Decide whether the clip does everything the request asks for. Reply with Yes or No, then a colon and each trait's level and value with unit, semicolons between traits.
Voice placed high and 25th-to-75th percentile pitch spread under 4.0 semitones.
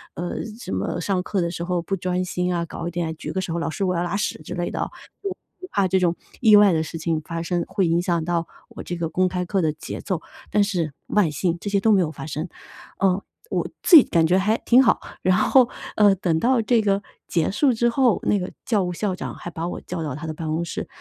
No: medium, 180 Hz; average, 3.3 semitones